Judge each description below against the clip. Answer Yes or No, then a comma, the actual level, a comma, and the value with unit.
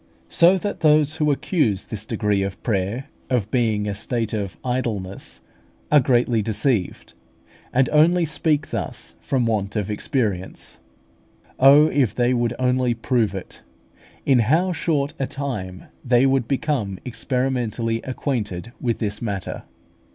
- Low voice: Yes, low, 120 Hz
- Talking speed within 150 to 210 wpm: No, slow, 135 wpm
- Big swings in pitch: No, average, 4.7 semitones